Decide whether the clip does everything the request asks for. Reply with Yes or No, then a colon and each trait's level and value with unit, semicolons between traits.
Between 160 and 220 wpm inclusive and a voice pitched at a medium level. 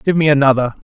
Yes: average, 200 wpm; medium, 145 Hz